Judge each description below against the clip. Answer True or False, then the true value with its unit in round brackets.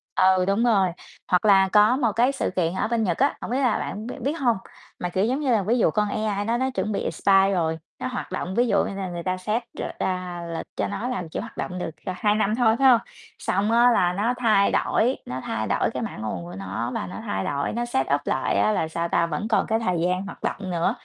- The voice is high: True (200 Hz)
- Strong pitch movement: False (4.6 semitones)